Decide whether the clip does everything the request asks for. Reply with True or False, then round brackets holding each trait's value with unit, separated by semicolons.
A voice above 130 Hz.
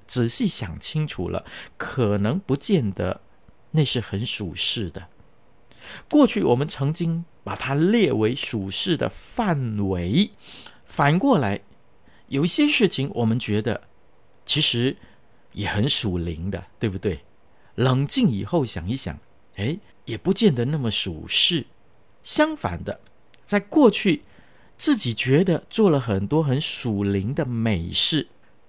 False (120 Hz)